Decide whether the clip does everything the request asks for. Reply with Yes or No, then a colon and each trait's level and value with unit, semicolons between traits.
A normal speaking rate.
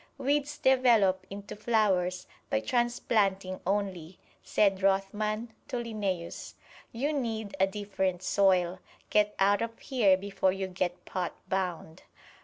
No: slow, 120 wpm